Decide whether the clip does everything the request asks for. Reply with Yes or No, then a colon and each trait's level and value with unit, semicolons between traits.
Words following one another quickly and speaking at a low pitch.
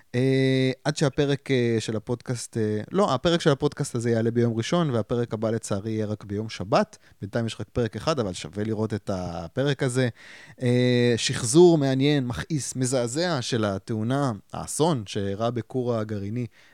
Yes: fast, 160 wpm; low, 120 Hz